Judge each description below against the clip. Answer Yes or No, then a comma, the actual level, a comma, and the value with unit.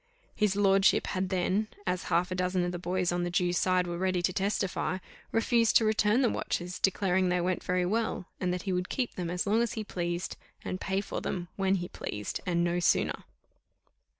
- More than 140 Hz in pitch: Yes, medium, 185 Hz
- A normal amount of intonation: No, narrow, 1.9 semitones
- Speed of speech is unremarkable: No, fast, 210 wpm